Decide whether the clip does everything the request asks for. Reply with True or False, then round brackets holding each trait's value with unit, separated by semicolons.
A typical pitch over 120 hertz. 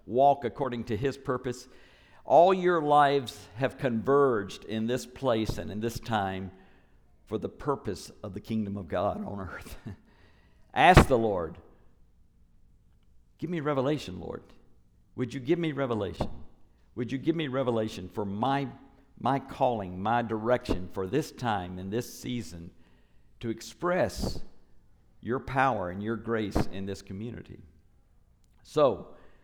False (115 Hz)